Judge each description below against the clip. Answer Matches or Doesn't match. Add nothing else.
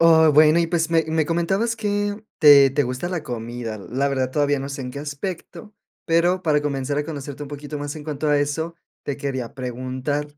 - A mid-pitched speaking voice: Matches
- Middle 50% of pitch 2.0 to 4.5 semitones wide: Matches